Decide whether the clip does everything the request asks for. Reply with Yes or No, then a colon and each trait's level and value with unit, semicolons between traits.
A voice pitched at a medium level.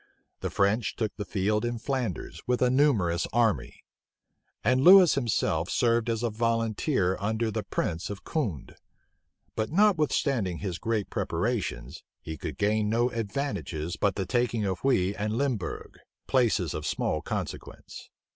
No: low, 110 Hz